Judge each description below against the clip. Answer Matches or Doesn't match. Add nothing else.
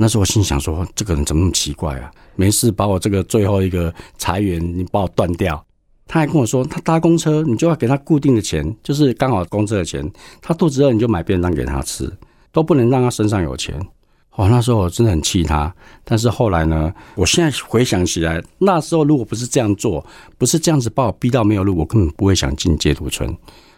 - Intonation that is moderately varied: Doesn't match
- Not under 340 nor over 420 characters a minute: Matches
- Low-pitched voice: Matches